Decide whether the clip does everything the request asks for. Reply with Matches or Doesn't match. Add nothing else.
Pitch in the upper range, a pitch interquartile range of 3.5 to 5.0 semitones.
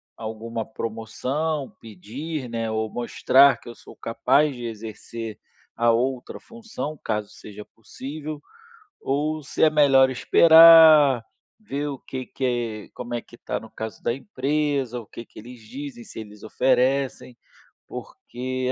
Doesn't match